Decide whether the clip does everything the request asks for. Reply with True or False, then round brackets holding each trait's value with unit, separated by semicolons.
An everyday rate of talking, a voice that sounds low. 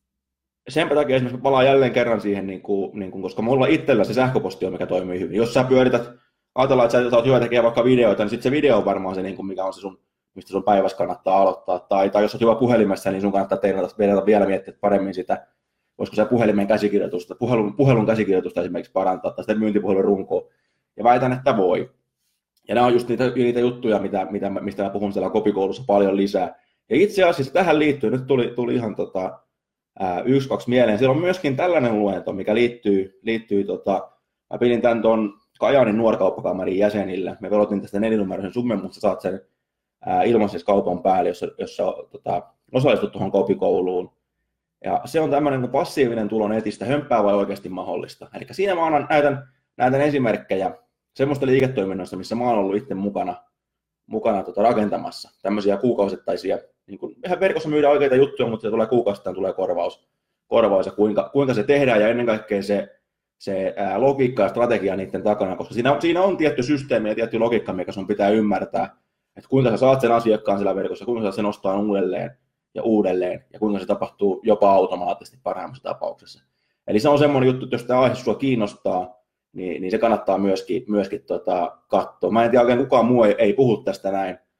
False (190 wpm; 110 Hz)